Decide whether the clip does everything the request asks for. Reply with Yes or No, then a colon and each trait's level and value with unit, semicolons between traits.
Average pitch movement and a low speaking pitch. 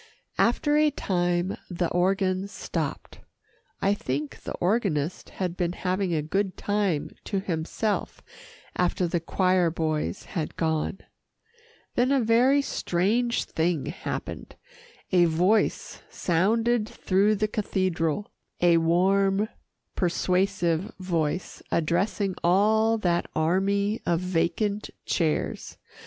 No: average, 3.3 semitones; medium, 185 Hz